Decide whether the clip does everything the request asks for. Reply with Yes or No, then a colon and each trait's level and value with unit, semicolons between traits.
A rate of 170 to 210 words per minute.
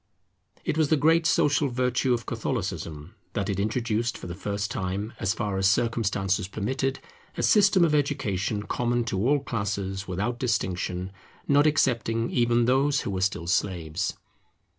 No: average, 155 wpm